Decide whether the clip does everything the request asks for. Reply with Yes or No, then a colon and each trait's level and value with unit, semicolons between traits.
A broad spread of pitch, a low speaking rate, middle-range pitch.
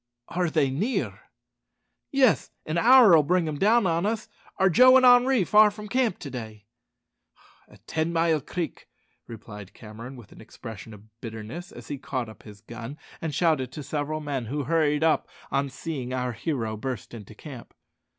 No: wide, 7.0 semitones; average, 170 wpm; medium, 150 Hz